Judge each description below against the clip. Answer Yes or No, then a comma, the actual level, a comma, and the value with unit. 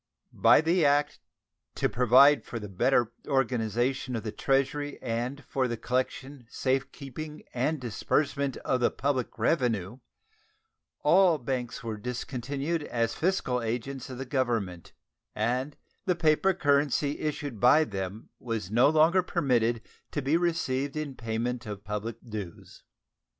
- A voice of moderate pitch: No, low, 130 Hz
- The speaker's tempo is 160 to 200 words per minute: No, slow, 135 wpm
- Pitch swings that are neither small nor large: Yes, average, 3.7 semitones